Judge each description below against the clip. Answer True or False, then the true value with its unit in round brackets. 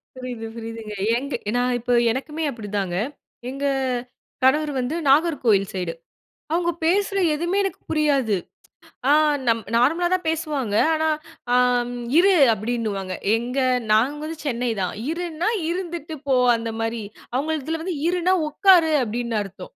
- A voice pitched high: True (270 Hz)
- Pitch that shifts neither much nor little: False (6.1 semitones)